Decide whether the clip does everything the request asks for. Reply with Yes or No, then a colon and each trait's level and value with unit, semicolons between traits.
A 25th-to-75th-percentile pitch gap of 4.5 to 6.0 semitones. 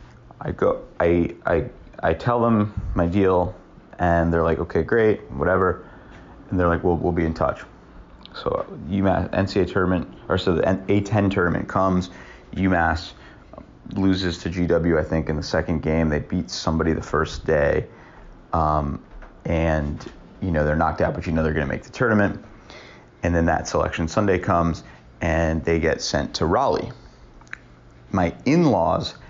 No: average, 2.9 semitones